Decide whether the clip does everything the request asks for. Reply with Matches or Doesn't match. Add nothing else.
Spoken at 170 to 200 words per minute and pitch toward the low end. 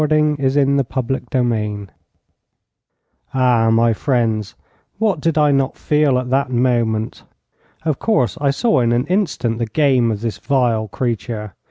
Doesn't match